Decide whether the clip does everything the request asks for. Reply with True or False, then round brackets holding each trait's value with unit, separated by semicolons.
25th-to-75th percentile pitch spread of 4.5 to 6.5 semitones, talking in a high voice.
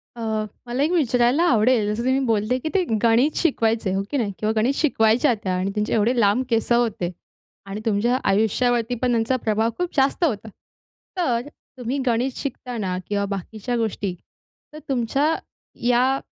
False (3.2 semitones; 235 Hz)